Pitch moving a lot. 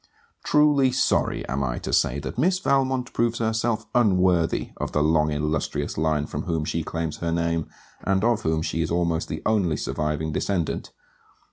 Yes: wide, 6.6 semitones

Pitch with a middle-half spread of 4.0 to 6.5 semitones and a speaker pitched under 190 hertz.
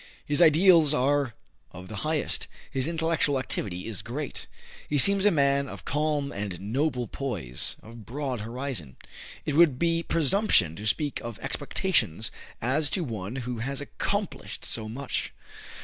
Yes: wide, 5.4 semitones; medium, 140 Hz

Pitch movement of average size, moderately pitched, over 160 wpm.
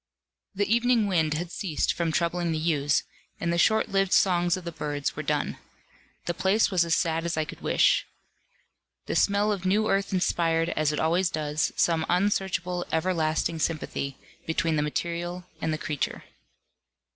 Yes: average, 3.0 semitones; medium, 170 Hz; average, 170 wpm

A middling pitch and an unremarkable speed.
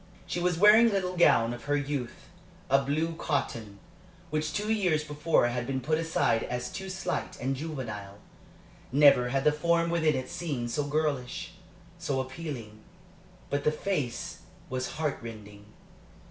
Yes: medium, 145 Hz; average, 155 wpm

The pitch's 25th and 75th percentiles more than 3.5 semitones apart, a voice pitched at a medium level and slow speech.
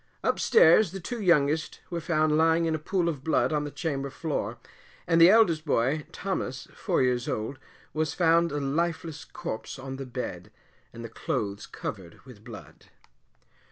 No: average, 4.3 semitones; medium, 155 Hz; average, 170 wpm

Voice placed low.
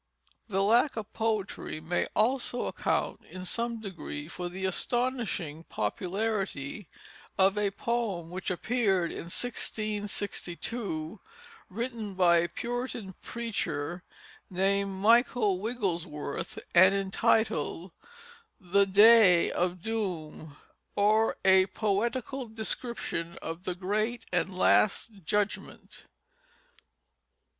No: high, 200 Hz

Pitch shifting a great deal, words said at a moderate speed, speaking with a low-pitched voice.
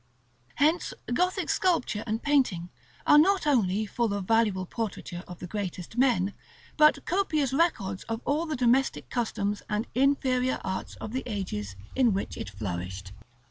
No: wide, 6.5 semitones; average, 150 wpm; high, 225 Hz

